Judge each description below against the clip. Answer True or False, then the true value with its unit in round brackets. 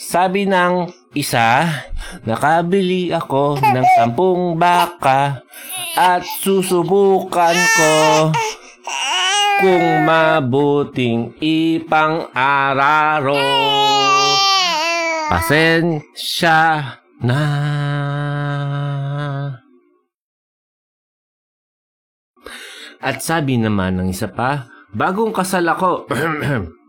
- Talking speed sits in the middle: False (55 wpm)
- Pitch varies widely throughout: False (4.6 semitones)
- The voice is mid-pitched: True (160 Hz)